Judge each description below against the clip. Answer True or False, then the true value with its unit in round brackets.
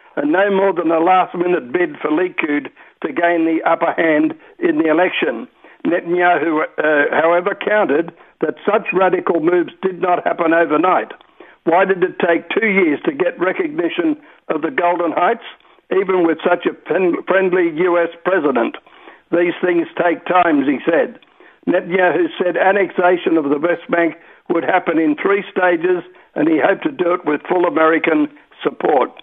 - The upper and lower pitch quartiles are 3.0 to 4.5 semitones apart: True (3.8 semitones)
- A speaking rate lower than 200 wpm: True (160 wpm)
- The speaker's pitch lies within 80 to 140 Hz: False (180 Hz)